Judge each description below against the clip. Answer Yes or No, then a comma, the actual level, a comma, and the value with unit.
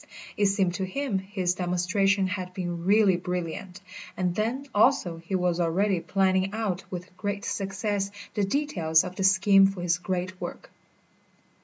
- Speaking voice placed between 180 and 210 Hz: Yes, high, 190 Hz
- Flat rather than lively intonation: Yes, narrow, 1.9 semitones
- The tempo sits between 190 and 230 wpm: No, average, 155 wpm